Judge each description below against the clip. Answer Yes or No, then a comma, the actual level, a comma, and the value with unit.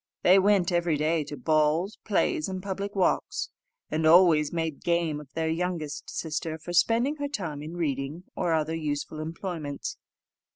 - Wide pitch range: No, average, 2.9 semitones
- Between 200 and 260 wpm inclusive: No, average, 160 wpm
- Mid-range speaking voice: Yes, medium, 165 Hz